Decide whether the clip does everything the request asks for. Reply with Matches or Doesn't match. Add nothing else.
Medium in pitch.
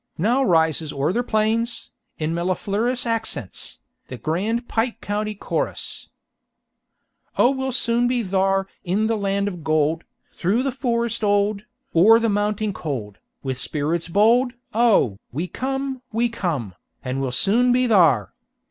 Doesn't match